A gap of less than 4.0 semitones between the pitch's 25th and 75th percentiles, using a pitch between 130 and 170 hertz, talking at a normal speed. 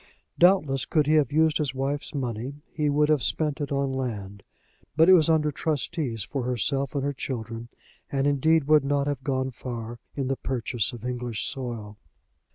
Yes: average, 3.5 semitones; low, 135 Hz; average, 180 wpm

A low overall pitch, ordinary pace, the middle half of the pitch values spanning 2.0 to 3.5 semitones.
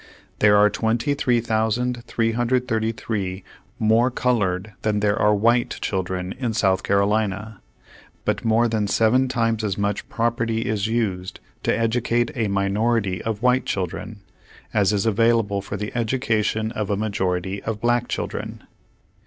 No: low, 110 Hz; slow, 130 wpm; narrow, 2.4 semitones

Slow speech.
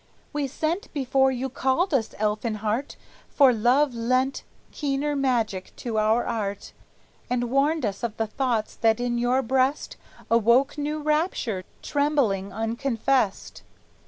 Yes: slow, 130 wpm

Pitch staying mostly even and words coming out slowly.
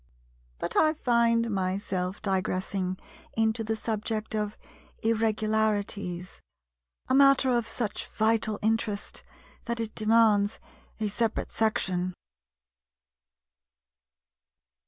Yes: narrow, 2.1 semitones; slow, 90 wpm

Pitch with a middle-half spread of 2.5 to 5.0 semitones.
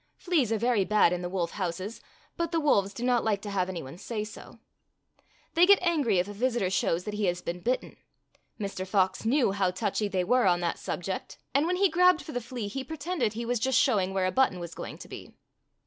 No: wide, 5.6 semitones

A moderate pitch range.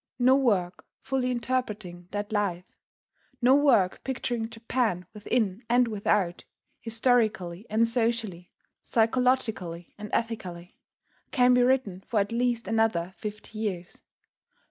Yes: average, 4.4 semitones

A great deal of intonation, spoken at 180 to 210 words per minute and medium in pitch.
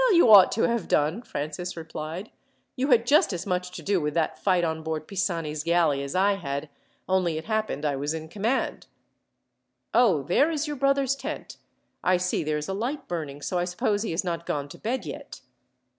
Yes: wide, 6.1 semitones; fast, 205 wpm; medium, 180 Hz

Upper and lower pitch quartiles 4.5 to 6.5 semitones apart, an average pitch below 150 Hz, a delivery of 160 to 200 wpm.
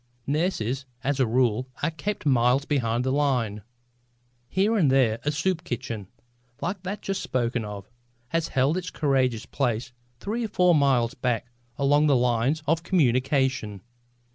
No: average, 4.9 semitones; low, 135 Hz; average, 150 wpm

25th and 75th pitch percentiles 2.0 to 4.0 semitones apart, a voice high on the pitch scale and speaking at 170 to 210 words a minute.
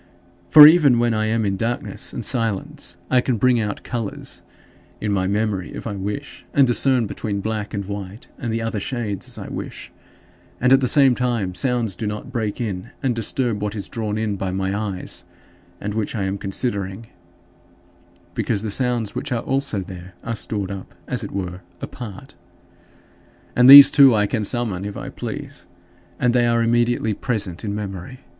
No: average, 3.5 semitones; low, 110 Hz; average, 185 wpm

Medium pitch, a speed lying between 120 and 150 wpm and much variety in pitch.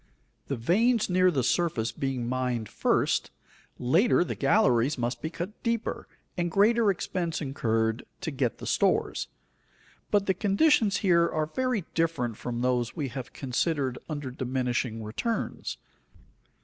Yes: medium, 145 Hz; slow, 135 wpm; wide, 7.3 semitones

